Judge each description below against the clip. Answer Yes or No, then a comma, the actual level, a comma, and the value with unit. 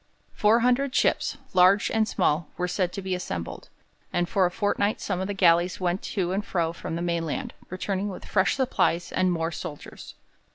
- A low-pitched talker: No, medium, 185 Hz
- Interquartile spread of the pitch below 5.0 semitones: Yes, average, 2.8 semitones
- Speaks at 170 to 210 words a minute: Yes, average, 180 wpm